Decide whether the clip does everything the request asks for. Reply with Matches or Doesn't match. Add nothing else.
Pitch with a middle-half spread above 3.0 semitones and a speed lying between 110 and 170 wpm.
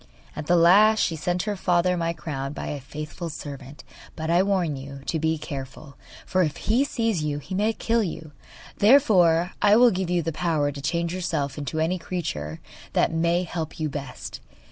Doesn't match